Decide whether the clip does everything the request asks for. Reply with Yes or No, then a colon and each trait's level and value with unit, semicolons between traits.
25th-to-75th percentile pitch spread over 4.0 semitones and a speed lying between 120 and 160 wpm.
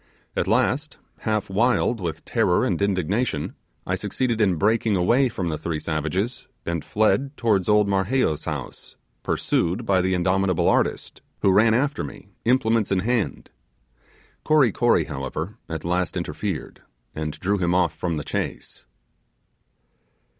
Yes: average, 5.1 semitones; average, 140 wpm